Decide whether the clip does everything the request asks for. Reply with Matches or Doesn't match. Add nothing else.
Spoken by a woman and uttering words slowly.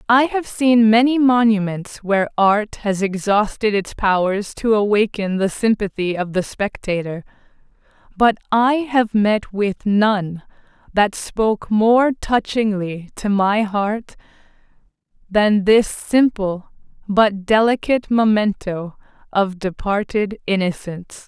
Matches